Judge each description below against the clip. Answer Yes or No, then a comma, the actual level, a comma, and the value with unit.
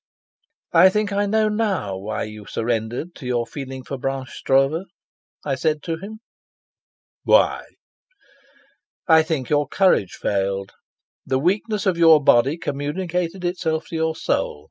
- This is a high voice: No, medium, 155 Hz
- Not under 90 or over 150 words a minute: Yes, average, 140 wpm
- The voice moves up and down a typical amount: No, wide, 5.9 semitones